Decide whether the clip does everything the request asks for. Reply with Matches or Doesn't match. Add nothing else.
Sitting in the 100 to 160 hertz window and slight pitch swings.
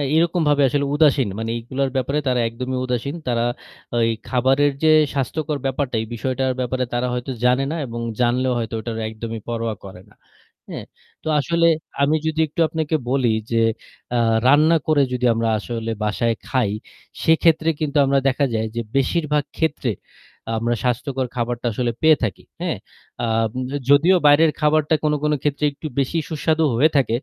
Doesn't match